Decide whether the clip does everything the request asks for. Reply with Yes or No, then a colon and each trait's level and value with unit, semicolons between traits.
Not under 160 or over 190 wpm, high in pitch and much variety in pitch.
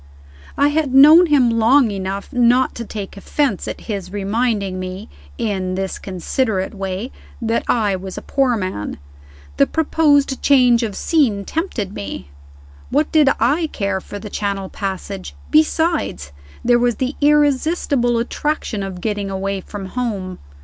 No: average, 145 wpm; high, 225 Hz; wide, 6.0 semitones